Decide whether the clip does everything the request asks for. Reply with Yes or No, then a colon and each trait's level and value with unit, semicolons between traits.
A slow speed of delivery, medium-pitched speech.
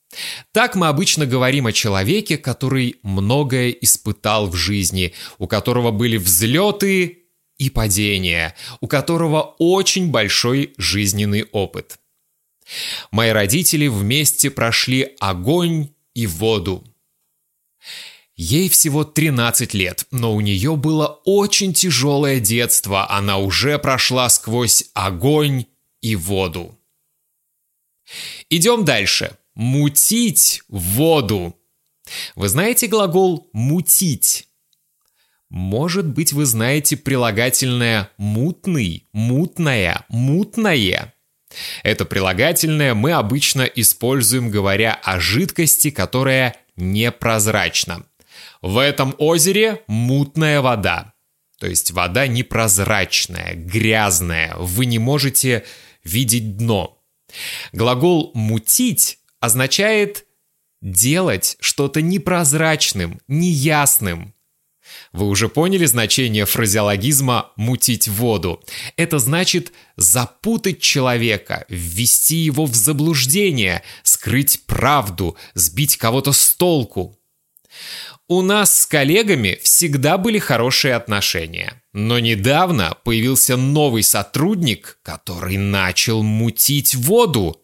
No: slow, 90 wpm; low, 125 Hz